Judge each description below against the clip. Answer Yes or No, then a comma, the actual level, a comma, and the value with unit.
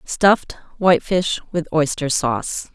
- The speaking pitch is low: No, medium, 165 Hz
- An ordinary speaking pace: No, slow, 110 wpm